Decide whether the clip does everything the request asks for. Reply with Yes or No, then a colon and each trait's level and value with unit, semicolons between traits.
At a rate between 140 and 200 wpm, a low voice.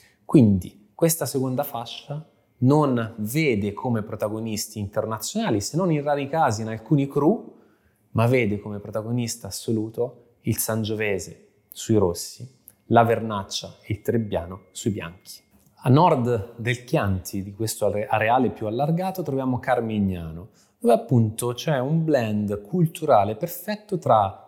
No: average, 125 wpm; low, 115 Hz